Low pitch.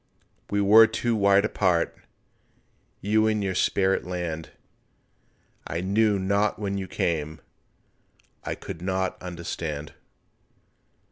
Yes: very low, 95 Hz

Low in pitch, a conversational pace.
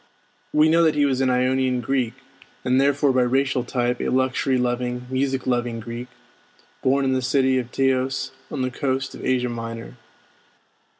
Yes: low, 130 Hz; average, 170 wpm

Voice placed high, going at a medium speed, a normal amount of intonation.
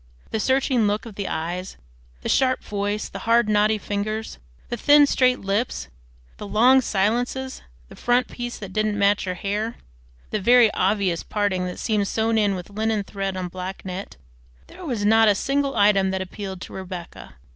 Yes: high, 210 Hz; average, 180 wpm; average, 3.1 semitones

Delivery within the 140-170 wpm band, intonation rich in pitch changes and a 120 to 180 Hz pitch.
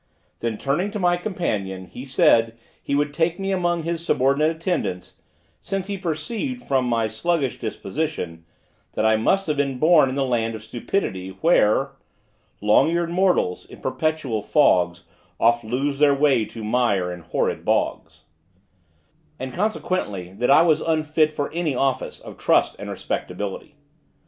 Yes: average, 155 wpm; wide, 7.1 semitones; medium, 140 Hz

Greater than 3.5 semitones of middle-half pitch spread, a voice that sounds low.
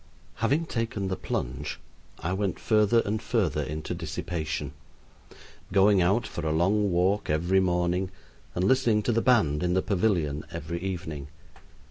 Yes: average, 4.3 semitones; very low, 95 Hz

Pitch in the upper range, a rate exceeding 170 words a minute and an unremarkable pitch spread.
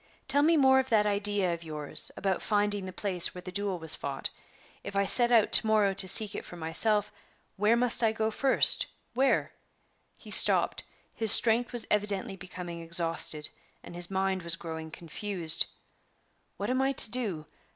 Yes: high, 200 Hz; average, 185 wpm; average, 4.3 semitones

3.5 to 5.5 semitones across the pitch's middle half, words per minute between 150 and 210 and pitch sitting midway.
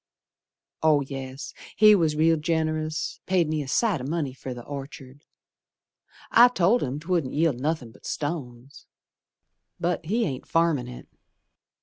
No: average, 3.8 semitones; average, 140 wpm; medium, 155 Hz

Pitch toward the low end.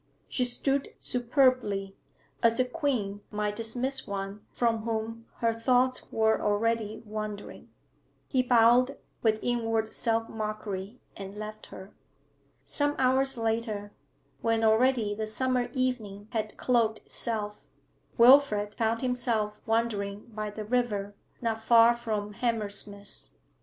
No: high, 225 Hz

